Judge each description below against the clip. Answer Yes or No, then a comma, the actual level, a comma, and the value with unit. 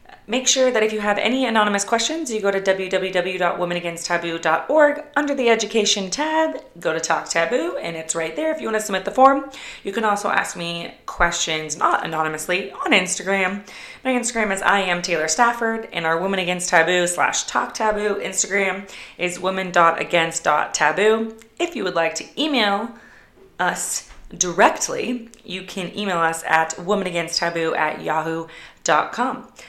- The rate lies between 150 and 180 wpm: Yes, average, 155 wpm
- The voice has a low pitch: No, high, 195 Hz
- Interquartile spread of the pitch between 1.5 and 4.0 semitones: No, average, 4.9 semitones